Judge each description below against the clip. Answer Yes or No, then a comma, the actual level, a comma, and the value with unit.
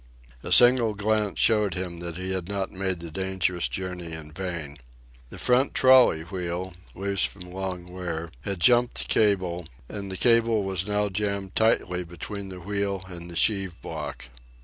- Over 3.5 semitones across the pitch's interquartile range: No, average, 2.8 semitones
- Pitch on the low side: Yes, very low, 95 Hz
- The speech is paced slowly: No, average, 170 wpm